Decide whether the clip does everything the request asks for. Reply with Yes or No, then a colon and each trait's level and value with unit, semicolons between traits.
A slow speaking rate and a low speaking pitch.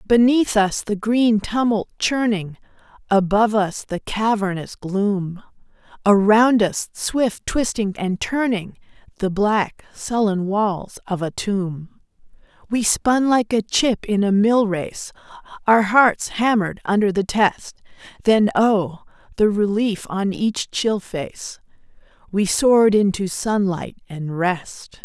No: slow, 120 wpm; high, 205 Hz